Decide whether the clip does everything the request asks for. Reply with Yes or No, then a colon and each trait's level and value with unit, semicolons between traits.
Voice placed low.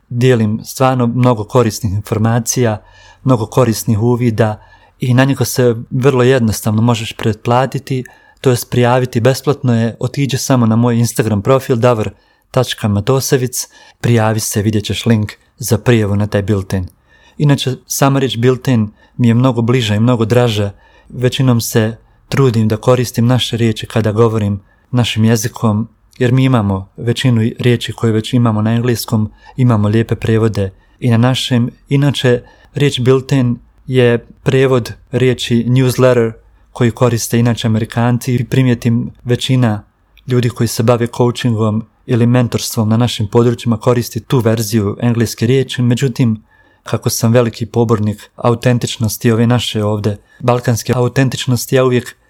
Yes: low, 120 Hz